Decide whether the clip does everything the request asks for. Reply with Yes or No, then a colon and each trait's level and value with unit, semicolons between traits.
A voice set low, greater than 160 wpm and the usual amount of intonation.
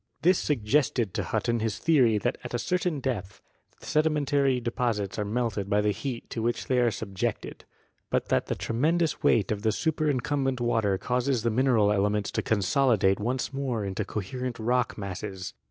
Yes: low, 120 Hz; average, 170 wpm; average, 4.3 semitones